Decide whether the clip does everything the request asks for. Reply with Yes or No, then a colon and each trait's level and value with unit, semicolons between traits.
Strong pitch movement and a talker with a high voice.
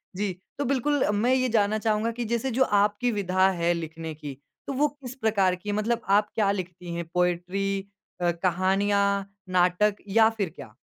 No: average, 3.9 semitones; high, 200 Hz